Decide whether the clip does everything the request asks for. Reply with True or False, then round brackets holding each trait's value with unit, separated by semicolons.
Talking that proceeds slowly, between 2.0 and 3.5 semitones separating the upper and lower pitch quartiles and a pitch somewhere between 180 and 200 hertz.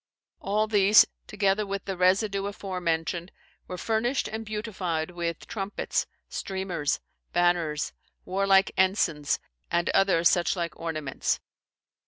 True (110 wpm; 2.9 semitones; 190 Hz)